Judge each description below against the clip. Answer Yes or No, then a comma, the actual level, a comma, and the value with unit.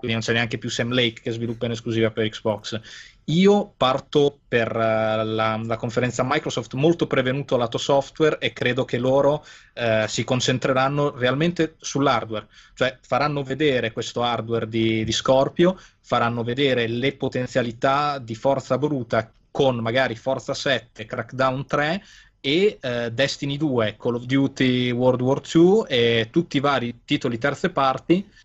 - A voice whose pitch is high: No, low, 130 Hz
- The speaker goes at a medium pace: Yes, average, 150 wpm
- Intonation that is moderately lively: Yes, average, 3.3 semitones